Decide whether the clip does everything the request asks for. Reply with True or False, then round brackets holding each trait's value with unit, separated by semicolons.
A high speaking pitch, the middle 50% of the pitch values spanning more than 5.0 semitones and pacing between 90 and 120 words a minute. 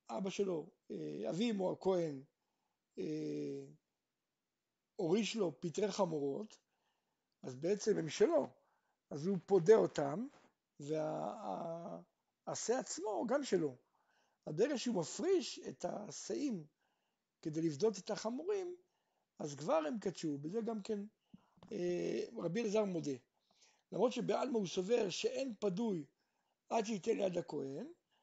True (200 Hz; 5.6 semitones; 115 wpm)